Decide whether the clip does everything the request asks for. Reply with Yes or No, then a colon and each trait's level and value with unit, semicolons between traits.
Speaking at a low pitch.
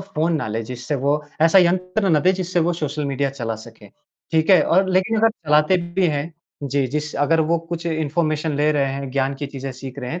No: medium, 150 Hz